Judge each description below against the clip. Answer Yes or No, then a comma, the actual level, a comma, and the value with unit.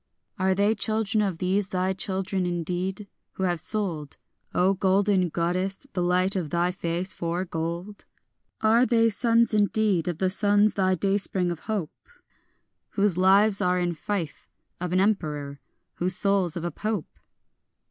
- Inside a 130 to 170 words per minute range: Yes, average, 155 wpm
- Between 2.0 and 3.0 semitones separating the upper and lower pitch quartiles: Yes, narrow, 2.6 semitones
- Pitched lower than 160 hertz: No, high, 190 Hz